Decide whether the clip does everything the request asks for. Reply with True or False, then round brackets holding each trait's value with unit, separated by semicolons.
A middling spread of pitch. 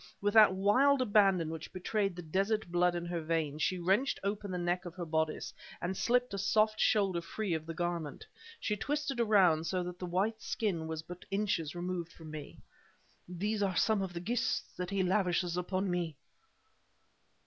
True (3.3 semitones)